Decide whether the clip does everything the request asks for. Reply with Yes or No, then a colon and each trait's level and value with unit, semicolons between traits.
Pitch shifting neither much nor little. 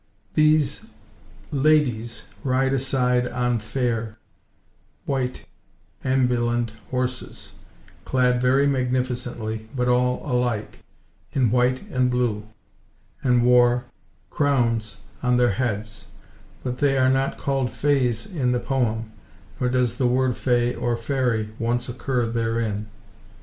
No: narrow, 1.7 semitones